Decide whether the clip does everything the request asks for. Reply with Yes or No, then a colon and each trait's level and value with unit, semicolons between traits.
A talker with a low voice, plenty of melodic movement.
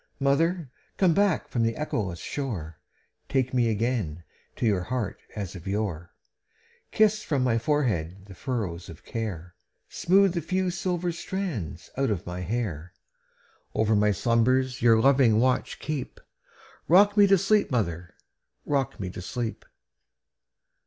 Yes: low, 120 Hz; wide, 8.1 semitones